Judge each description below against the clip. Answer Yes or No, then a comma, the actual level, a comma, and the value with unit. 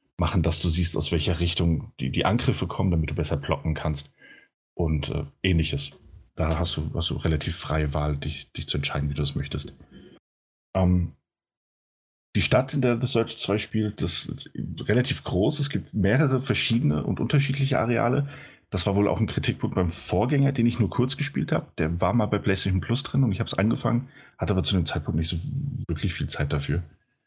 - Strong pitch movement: Yes, wide, 6.8 semitones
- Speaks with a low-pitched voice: Yes, very low, 95 Hz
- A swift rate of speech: Yes, fast, 200 wpm